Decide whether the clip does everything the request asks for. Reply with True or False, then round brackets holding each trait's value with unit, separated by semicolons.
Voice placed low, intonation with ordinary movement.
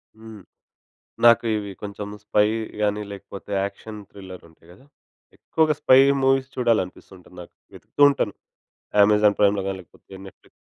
False (105 Hz; 2.3 semitones)